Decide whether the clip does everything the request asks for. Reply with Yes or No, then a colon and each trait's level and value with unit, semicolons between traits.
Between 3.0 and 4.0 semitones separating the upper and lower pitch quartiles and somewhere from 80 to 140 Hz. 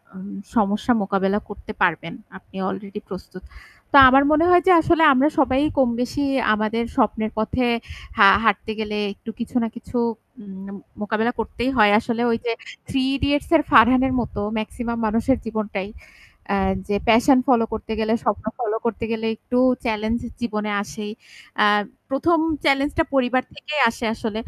No: average, 3.5 semitones; high, 225 Hz